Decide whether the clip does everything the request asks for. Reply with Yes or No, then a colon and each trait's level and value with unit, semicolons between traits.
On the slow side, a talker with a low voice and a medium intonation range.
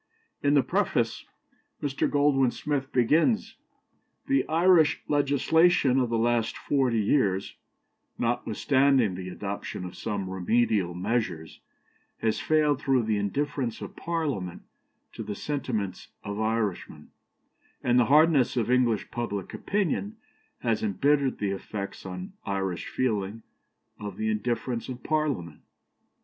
No: slow, 120 wpm; low, 120 Hz; wide, 5.8 semitones